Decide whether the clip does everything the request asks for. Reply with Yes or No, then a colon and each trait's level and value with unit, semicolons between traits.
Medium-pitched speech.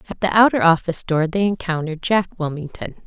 Yes: medium, 175 Hz